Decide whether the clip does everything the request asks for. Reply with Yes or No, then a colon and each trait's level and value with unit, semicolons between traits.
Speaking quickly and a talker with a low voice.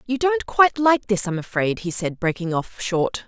No: fast, 220 wpm; high, 215 Hz